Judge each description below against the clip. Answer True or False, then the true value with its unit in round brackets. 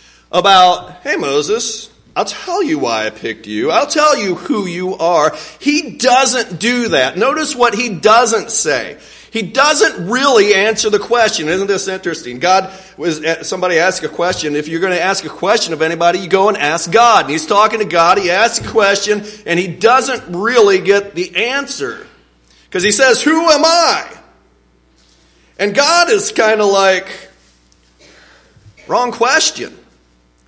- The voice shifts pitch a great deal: True (6.7 semitones)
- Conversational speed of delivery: True (165 wpm)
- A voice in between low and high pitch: False (195 Hz)